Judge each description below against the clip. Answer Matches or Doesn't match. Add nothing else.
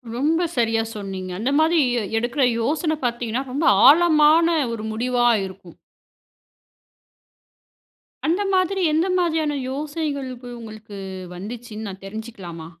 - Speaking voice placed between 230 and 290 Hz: Matches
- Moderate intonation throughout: Doesn't match